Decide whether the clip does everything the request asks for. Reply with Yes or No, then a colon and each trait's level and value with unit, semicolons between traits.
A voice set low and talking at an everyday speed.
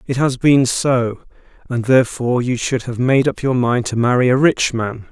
No: low, 125 Hz; fast, 210 wpm